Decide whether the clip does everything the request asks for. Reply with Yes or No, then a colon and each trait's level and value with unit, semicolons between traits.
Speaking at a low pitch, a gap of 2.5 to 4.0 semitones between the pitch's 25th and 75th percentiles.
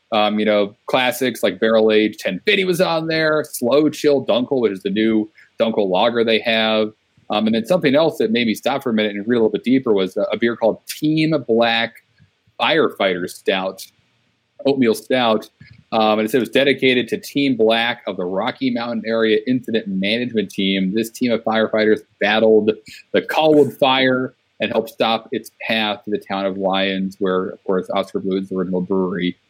Yes: low, 110 Hz; average, 3.3 semitones